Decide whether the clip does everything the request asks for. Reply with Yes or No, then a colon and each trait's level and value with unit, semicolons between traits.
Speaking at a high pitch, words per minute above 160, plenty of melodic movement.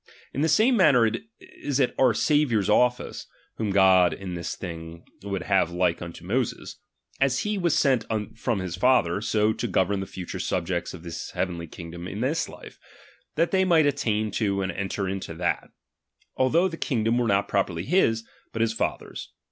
No: low, 105 Hz; average, 180 wpm; wide, 6.3 semitones